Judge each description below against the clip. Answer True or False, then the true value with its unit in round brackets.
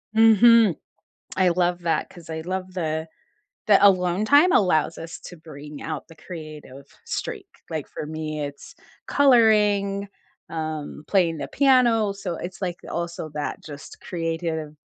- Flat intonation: False (4.1 semitones)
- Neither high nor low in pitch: True (175 Hz)